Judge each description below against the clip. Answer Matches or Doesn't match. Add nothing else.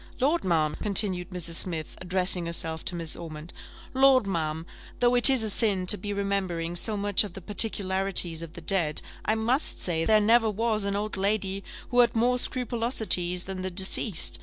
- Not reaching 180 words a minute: Doesn't match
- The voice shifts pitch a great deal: Doesn't match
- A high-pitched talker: Matches